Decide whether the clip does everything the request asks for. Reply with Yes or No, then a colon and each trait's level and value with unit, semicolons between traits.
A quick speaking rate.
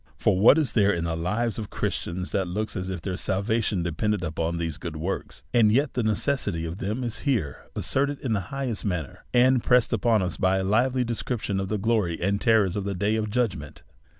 Yes: fast, 220 wpm